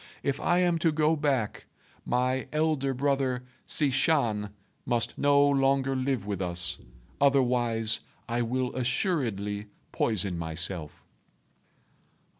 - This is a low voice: Yes, low, 130 Hz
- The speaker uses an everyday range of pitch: Yes, average, 4.8 semitones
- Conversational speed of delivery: No, slow, 110 wpm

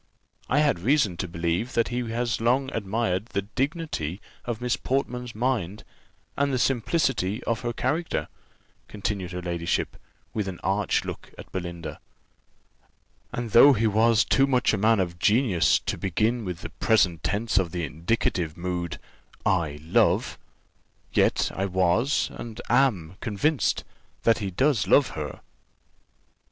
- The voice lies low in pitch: Yes, low, 110 Hz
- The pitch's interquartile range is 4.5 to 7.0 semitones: Yes, wide, 5.4 semitones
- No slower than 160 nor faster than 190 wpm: No, average, 145 wpm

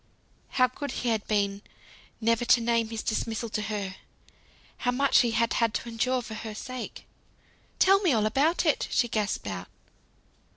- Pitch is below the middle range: No, high, 230 Hz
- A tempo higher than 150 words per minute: Yes, average, 170 wpm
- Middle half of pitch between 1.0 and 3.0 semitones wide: Yes, average, 2.7 semitones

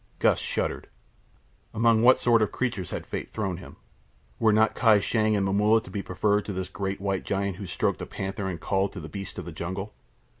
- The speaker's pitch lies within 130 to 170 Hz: No, low, 100 Hz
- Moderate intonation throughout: No, narrow, 2.2 semitones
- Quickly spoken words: Yes, fast, 215 wpm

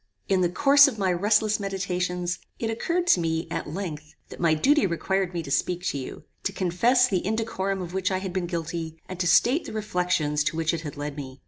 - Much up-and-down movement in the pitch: No, average, 3.6 semitones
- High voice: No, medium, 180 Hz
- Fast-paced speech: Yes, fast, 225 wpm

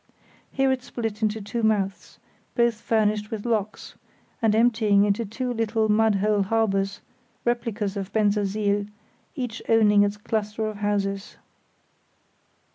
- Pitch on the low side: No, high, 215 Hz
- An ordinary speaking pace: No, slow, 125 wpm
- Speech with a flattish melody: Yes, narrow, 1.7 semitones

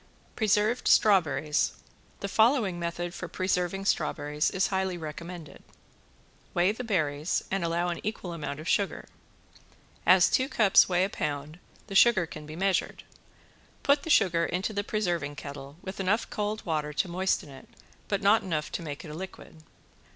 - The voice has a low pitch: No, medium, 180 Hz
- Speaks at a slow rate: No, average, 160 wpm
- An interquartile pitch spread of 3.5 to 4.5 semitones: Yes, average, 4.1 semitones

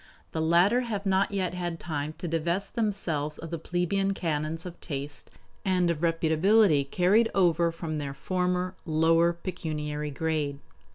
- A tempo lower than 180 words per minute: Yes, average, 150 wpm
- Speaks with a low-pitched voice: No, medium, 170 Hz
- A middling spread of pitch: Yes, average, 3.0 semitones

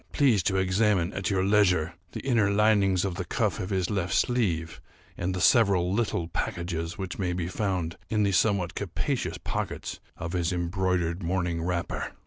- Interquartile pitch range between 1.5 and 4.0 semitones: Yes, narrow, 2.6 semitones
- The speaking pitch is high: No, very low, 95 Hz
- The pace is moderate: Yes, average, 170 wpm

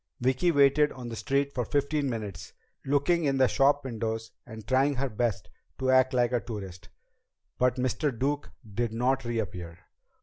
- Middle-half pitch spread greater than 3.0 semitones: Yes, average, 3.6 semitones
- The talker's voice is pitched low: Yes, low, 125 Hz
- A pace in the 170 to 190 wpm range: No, average, 160 wpm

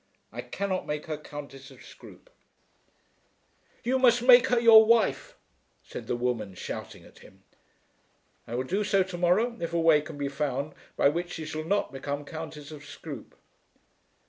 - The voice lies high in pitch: No, medium, 160 Hz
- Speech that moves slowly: No, average, 170 wpm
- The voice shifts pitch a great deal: Yes, wide, 5.9 semitones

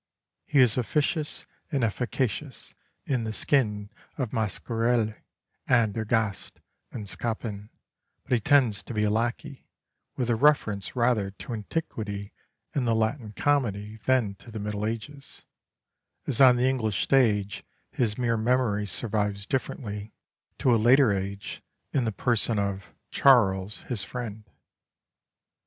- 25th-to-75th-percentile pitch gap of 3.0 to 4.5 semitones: Yes, average, 3.3 semitones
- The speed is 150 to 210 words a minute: No, slow, 135 wpm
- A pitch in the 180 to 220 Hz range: No, low, 115 Hz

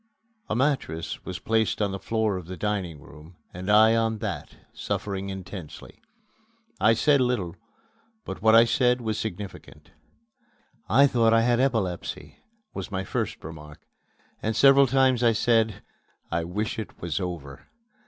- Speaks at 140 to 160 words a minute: Yes, average, 150 wpm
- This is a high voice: No, low, 105 Hz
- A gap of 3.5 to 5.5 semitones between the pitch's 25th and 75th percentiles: Yes, average, 4.2 semitones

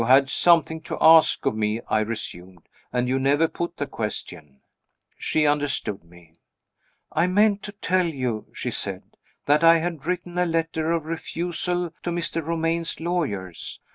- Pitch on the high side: No, medium, 160 Hz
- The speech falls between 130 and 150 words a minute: No, average, 160 wpm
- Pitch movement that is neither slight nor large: No, wide, 5.8 semitones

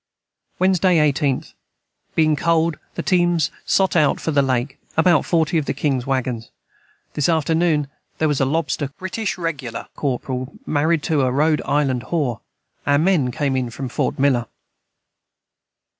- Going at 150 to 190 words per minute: No, average, 140 wpm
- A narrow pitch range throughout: No, average, 3.7 semitones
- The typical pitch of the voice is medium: Yes, medium, 150 Hz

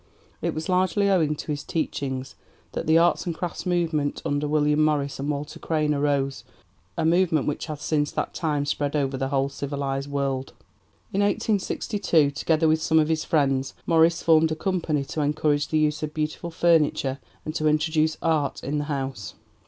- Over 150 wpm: Yes, average, 180 wpm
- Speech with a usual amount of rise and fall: No, narrow, 2.2 semitones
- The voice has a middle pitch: Yes, medium, 150 Hz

